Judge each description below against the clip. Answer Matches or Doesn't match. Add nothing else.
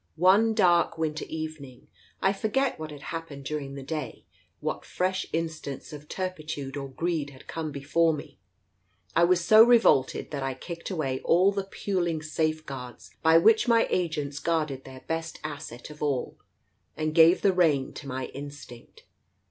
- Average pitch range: Matches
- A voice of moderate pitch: Matches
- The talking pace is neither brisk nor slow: Matches